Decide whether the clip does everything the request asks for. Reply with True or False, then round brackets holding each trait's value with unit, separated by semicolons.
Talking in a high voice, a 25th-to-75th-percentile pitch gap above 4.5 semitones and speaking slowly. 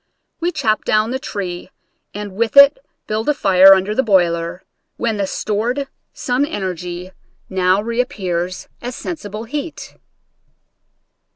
True (210 Hz; 5.0 semitones; 130 wpm)